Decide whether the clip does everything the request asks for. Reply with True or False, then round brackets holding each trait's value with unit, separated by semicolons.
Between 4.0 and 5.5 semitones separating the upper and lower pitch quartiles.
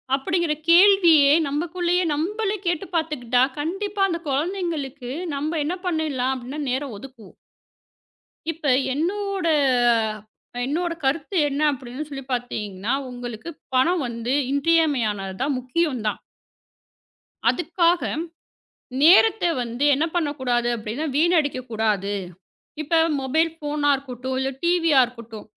True (5.2 semitones)